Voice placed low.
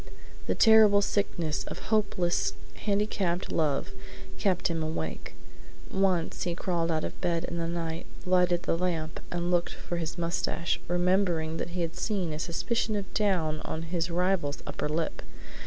No: medium, 175 Hz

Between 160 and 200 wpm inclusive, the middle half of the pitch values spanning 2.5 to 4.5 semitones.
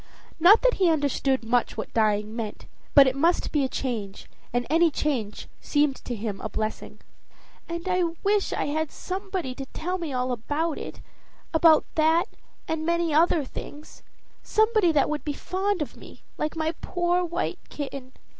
No: average, 170 wpm; average, 5.0 semitones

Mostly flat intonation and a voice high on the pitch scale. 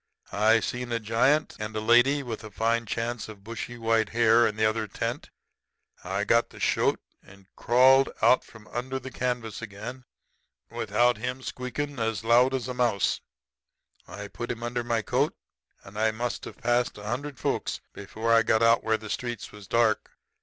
No: narrow, 2.0 semitones; low, 115 Hz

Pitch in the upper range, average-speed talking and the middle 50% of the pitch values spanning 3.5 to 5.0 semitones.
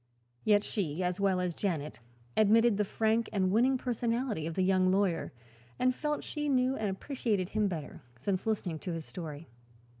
Yes: high, 200 Hz; average, 175 wpm; average, 4.3 semitones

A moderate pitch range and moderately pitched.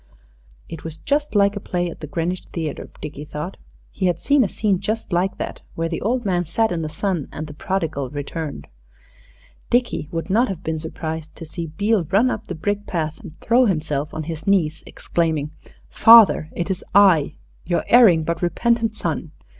Yes: average, 4.4 semitones; medium, 175 Hz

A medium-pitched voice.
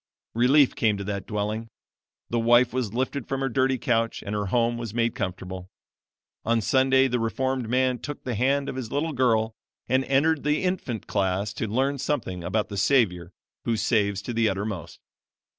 No: low, 115 Hz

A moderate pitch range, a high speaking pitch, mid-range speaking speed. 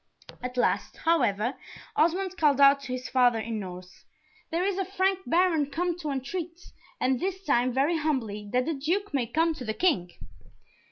No: wide, 5.9 semitones; very high, 285 Hz; average, 175 wpm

